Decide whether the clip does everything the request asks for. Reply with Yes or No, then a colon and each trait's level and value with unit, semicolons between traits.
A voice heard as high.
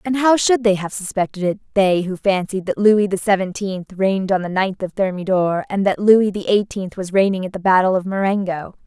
Yes: high, 195 Hz